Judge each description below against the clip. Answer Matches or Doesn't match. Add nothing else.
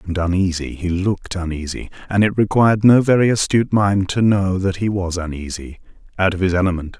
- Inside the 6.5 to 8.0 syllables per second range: Matches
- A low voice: Matches